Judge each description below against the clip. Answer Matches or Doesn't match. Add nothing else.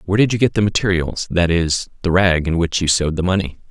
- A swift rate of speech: Matches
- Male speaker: Matches